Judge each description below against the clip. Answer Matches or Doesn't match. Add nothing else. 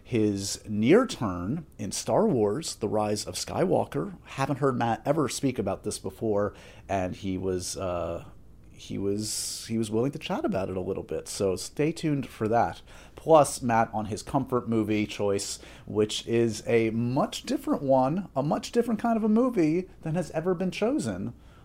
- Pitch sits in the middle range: Doesn't match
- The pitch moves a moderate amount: Doesn't match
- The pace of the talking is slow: Doesn't match